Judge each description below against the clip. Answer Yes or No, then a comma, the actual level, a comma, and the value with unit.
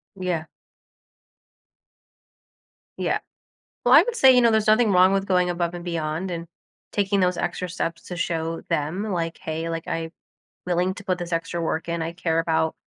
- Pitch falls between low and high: Yes, medium, 175 Hz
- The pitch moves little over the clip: Yes, narrow, 2.0 semitones